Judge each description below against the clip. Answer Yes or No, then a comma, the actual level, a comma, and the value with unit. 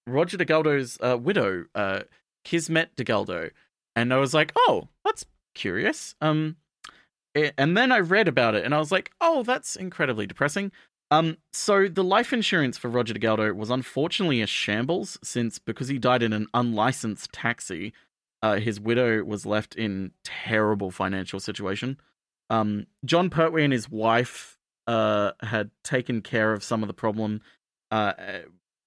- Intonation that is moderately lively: No, wide, 6.9 semitones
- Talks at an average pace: Yes, average, 155 wpm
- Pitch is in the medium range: No, low, 125 Hz